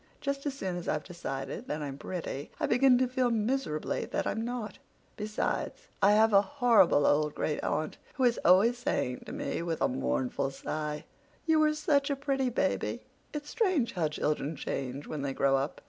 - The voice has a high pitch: Yes, high, 205 Hz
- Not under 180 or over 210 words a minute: Yes, average, 185 wpm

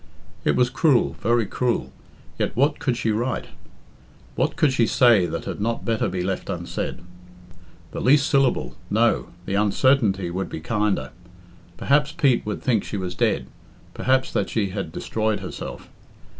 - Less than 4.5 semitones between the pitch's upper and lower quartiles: No, average, 5.1 semitones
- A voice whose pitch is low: Yes, low, 115 Hz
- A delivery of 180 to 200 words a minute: No, average, 155 wpm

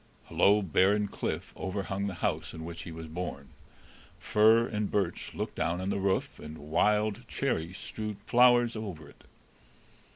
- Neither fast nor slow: Yes, average, 160 wpm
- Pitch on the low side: Yes, low, 100 Hz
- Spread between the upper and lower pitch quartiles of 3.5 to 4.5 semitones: Yes, average, 4.2 semitones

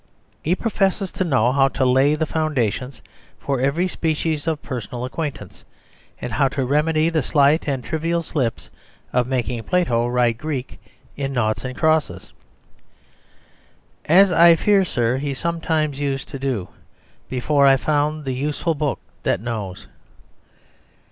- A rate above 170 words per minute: No, average, 140 wpm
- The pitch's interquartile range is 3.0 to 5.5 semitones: Yes, average, 3.9 semitones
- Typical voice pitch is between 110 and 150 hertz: Yes, medium, 140 Hz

